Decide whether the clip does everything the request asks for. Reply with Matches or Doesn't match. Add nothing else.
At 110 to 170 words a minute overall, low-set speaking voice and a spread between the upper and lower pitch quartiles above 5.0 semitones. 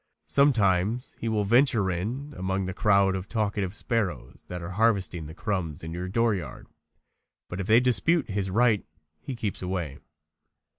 Doesn't match